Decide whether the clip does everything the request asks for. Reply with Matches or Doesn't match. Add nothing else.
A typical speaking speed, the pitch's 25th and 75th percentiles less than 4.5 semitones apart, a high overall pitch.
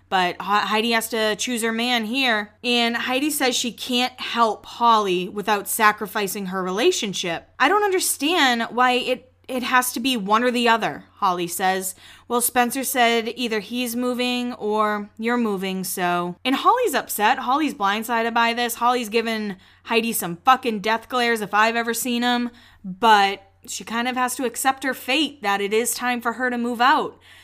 Matches